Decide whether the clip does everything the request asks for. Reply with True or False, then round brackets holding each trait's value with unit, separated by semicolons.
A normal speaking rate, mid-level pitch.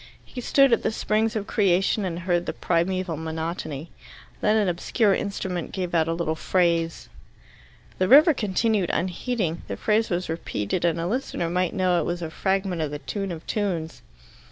True (180 wpm; 180 Hz)